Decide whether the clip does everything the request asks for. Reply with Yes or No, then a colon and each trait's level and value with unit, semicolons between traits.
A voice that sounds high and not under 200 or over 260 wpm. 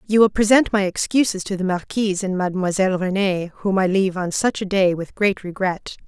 Yes: high, 195 Hz; fast, 205 wpm